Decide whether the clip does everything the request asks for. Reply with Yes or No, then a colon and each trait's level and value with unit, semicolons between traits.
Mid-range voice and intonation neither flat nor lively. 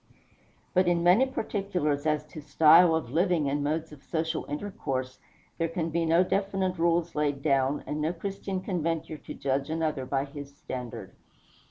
Yes: medium, 160 Hz; average, 3.5 semitones